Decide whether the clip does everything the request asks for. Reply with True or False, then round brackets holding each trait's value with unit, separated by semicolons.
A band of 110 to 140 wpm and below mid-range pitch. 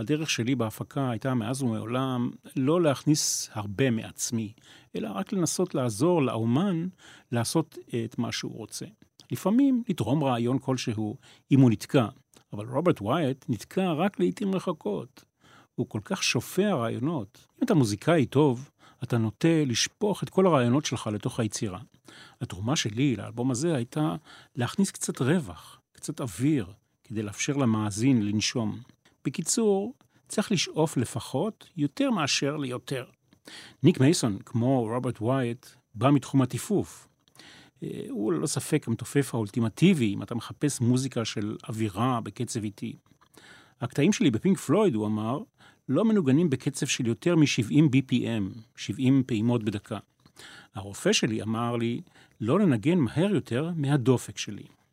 True (130 wpm; 130 Hz)